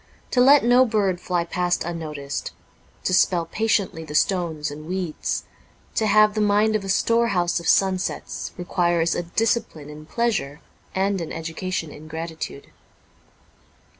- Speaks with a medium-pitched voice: Yes, medium, 180 Hz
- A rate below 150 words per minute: Yes, slow, 135 wpm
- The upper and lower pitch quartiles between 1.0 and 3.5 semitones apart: No, average, 4.3 semitones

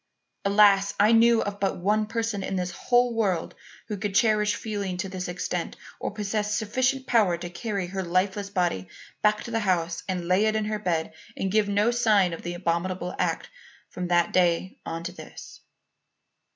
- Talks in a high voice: Yes, high, 200 Hz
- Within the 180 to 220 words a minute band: Yes, average, 190 wpm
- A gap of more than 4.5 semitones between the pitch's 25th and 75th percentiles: No, average, 3.0 semitones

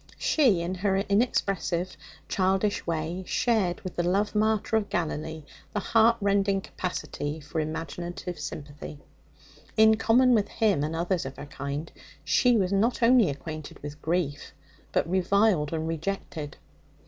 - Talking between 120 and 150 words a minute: Yes, slow, 135 wpm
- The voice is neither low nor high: Yes, medium, 180 Hz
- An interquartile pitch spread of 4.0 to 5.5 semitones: Yes, average, 4.7 semitones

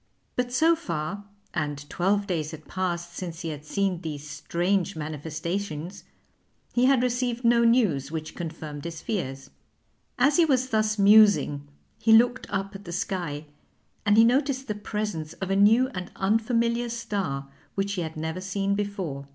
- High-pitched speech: Yes, high, 195 Hz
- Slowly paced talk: No, average, 160 wpm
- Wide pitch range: Yes, wide, 6.0 semitones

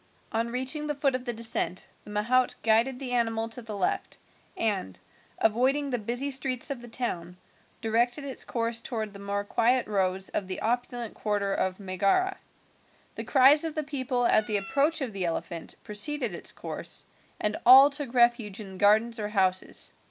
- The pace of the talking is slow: No, average, 175 wpm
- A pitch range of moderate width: Yes, average, 4.0 semitones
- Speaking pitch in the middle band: No, high, 230 Hz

